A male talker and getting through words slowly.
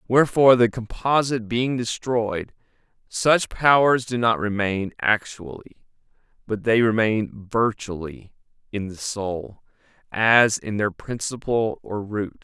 Yes: male; slow, 115 wpm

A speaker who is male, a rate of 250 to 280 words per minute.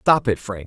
Yes: male; fast, 270 wpm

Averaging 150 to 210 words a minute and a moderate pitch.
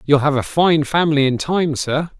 No: fast, 220 wpm; medium, 150 Hz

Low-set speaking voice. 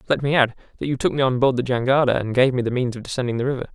Yes: low, 125 Hz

